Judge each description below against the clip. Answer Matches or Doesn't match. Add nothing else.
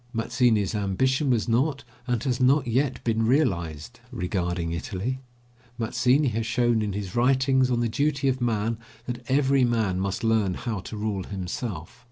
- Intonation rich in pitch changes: Doesn't match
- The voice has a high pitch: Doesn't match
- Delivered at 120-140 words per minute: Doesn't match